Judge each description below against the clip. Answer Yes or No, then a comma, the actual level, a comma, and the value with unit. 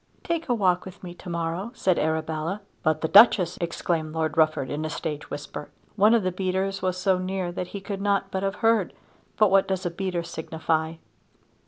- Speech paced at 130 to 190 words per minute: No, average, 200 wpm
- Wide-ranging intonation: No, average, 3.4 semitones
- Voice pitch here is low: No, medium, 180 Hz